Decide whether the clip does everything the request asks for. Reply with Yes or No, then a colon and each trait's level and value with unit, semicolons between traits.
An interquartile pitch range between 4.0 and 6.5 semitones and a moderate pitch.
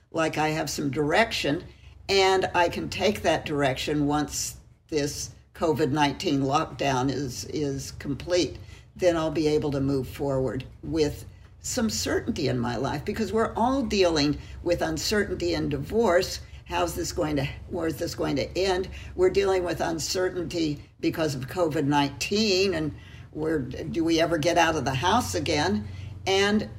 Yes: average, 4.3 semitones; medium, 155 Hz